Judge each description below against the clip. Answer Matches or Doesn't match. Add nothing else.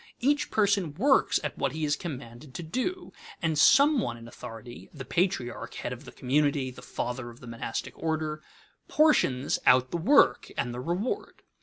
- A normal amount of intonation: Doesn't match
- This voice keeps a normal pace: Matches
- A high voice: Doesn't match